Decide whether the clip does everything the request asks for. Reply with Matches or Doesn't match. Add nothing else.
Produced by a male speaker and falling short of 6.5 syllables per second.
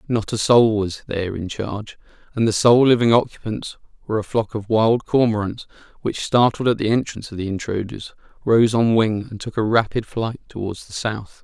Matches